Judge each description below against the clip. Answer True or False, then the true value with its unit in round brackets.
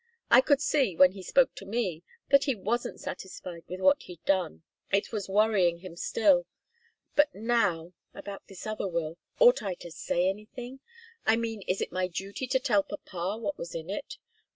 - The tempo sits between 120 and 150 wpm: False (185 wpm)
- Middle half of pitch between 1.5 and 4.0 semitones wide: False (4.9 semitones)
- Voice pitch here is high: True (200 Hz)